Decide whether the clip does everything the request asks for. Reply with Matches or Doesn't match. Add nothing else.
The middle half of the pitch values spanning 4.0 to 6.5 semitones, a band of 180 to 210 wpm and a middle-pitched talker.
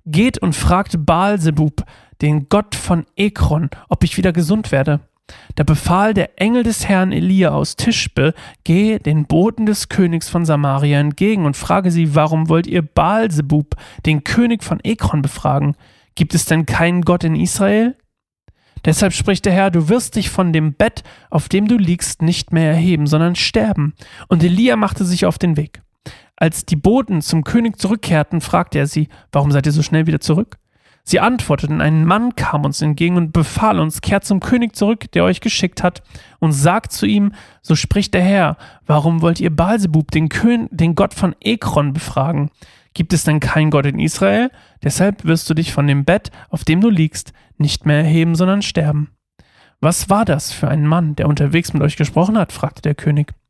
Matches